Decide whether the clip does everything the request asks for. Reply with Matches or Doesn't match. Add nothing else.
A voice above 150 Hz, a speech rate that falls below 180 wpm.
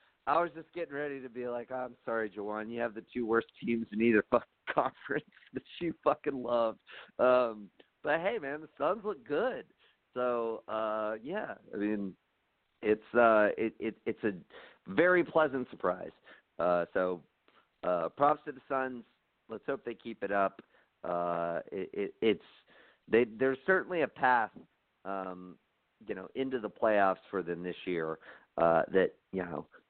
Doesn't match